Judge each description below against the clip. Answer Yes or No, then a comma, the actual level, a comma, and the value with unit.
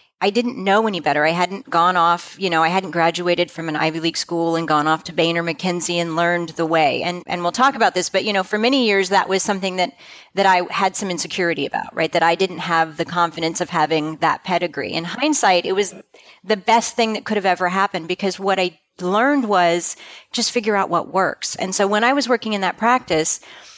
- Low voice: No, medium, 180 Hz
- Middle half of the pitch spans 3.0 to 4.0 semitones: Yes, average, 3.5 semitones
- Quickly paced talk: Yes, fast, 235 wpm